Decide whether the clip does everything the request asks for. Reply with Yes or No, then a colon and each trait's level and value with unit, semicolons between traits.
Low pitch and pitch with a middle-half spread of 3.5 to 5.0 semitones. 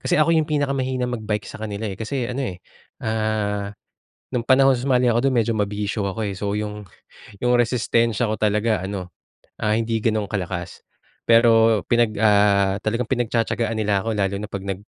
No: low, 110 Hz; average, 2.8 semitones